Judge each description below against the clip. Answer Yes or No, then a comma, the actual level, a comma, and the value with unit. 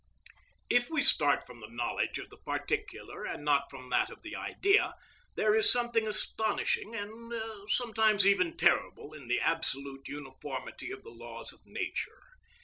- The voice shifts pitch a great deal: Yes, wide, 9.0 semitones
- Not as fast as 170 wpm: Yes, average, 155 wpm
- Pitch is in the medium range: No, high, 200 Hz